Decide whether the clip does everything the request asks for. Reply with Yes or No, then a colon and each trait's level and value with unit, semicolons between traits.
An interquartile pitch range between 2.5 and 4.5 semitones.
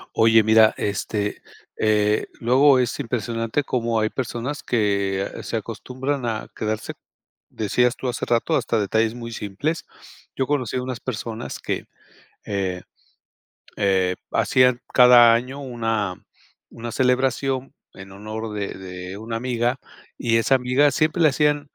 Yes: average, 3.1 semitones